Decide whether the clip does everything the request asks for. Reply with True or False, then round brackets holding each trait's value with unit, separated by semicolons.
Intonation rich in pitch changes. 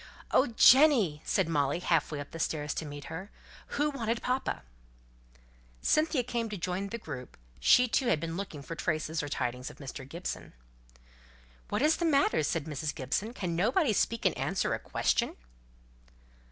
True (7.9 semitones)